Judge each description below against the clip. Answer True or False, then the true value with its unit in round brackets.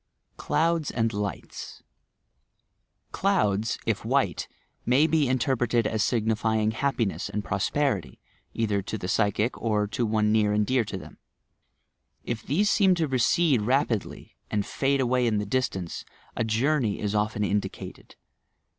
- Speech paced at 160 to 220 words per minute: False (135 wpm)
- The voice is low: True (115 Hz)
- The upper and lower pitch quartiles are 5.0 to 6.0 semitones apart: False (4.2 semitones)